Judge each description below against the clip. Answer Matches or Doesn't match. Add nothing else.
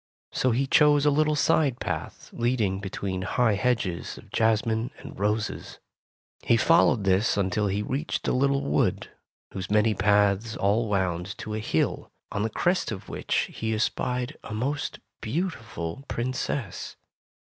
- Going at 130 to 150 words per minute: Matches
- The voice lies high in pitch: Doesn't match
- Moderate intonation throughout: Matches